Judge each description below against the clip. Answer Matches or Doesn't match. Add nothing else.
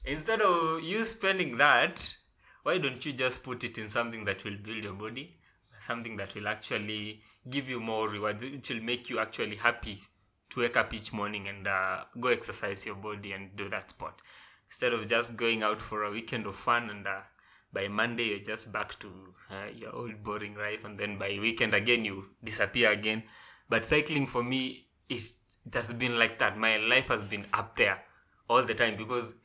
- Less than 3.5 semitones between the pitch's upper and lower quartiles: Matches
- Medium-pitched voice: Doesn't match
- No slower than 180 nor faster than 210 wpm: Matches